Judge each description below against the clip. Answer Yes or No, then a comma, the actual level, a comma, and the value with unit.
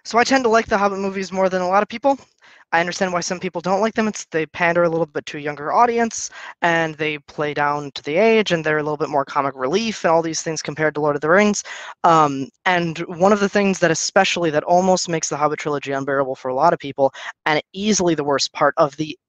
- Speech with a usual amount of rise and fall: Yes, average, 4.3 semitones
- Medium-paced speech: No, fast, 260 wpm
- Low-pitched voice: No, medium, 170 Hz